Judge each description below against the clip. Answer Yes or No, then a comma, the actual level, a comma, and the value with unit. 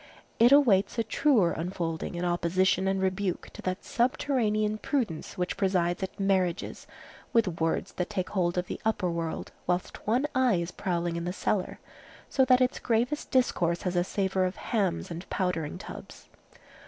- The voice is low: No, high, 190 Hz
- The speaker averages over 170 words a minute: No, average, 165 wpm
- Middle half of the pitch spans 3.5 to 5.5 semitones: Yes, average, 4.0 semitones